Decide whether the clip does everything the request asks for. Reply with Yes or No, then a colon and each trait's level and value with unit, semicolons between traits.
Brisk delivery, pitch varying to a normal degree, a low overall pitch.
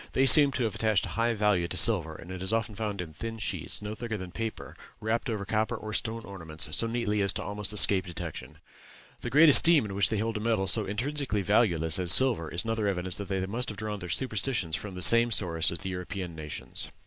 Yes: fast, 235 wpm; average, 3.7 semitones; low, 105 Hz